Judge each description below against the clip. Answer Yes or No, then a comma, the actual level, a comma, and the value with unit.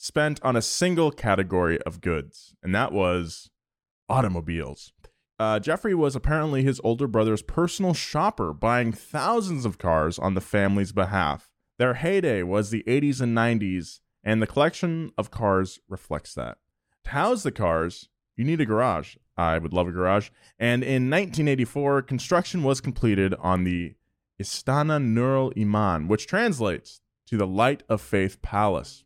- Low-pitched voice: Yes, low, 115 Hz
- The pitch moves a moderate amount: No, wide, 6.8 semitones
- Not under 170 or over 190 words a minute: No, average, 155 wpm